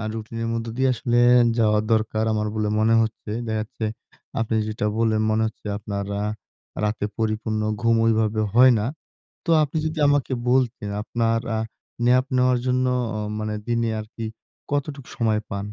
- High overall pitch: No, low, 115 Hz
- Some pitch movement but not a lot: No, narrow, 2.3 semitones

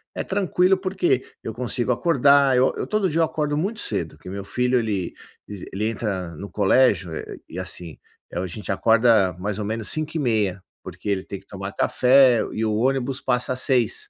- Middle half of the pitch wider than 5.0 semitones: Yes, wide, 5.4 semitones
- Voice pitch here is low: Yes, low, 115 Hz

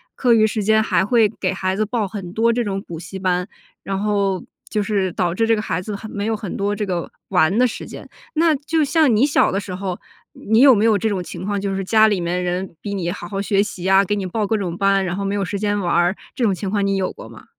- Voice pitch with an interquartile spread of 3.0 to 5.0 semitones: No, narrow, 2.6 semitones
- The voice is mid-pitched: No, high, 200 Hz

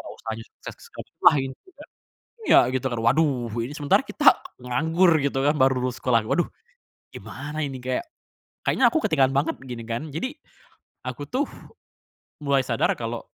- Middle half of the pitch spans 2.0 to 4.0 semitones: Yes, average, 3.7 semitones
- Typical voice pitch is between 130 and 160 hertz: Yes, low, 135 Hz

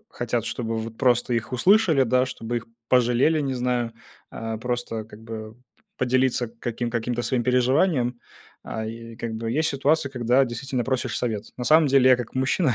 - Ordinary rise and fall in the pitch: No, narrow, 2.2 semitones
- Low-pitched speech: Yes, low, 125 Hz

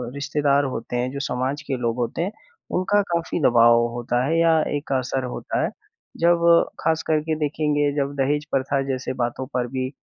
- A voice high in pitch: No, medium, 140 Hz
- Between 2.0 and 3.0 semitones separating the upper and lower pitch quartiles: No, average, 3.5 semitones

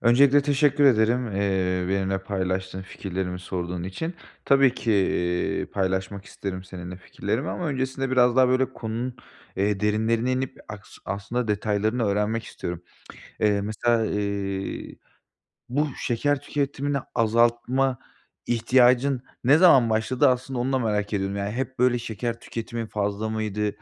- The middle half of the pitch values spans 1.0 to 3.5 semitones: No, average, 4.3 semitones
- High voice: No, low, 110 Hz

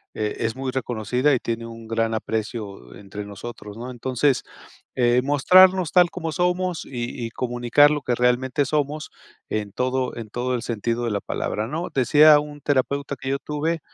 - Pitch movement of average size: Yes, average, 4.2 semitones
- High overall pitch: No, low, 125 Hz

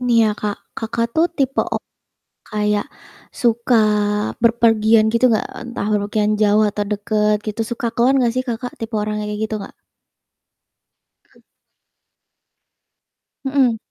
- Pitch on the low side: No, high, 220 Hz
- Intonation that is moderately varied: No, narrow, 2.0 semitones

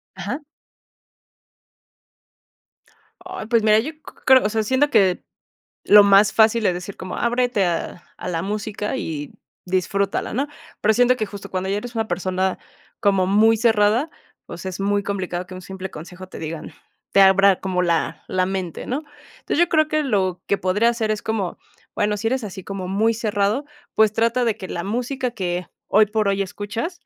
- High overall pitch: Yes, high, 205 Hz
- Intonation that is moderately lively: Yes, average, 3.5 semitones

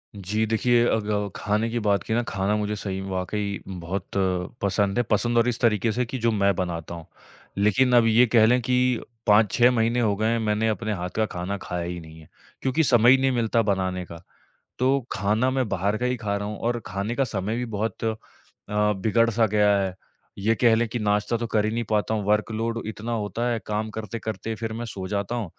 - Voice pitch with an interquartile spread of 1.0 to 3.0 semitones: Yes, narrow, 2.6 semitones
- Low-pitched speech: Yes, low, 110 Hz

